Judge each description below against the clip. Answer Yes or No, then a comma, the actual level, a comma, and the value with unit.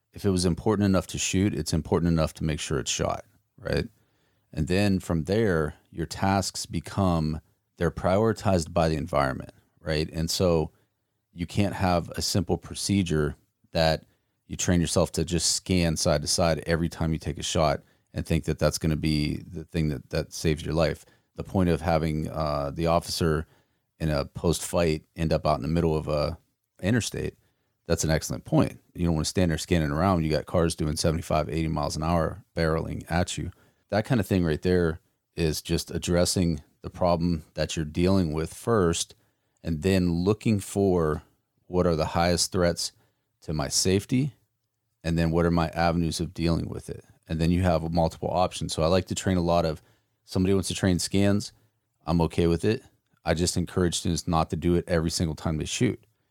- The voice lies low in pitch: Yes, very low, 85 Hz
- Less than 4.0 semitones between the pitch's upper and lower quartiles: Yes, average, 3.3 semitones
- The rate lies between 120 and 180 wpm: No, average, 195 wpm